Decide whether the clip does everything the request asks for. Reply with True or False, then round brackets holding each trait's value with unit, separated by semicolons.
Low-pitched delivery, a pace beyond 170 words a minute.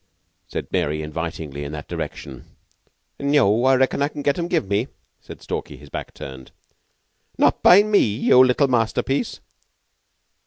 False (115 Hz; 145 wpm)